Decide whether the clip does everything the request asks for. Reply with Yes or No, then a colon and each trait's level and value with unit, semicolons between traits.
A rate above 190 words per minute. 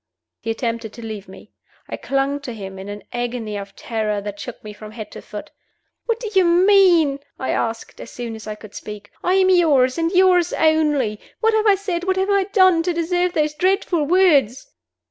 Yes: fast, 205 wpm